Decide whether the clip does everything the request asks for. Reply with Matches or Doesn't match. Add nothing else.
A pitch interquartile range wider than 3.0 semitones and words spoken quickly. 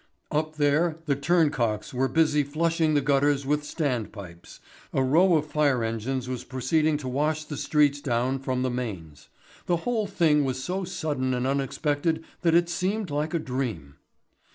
Doesn't match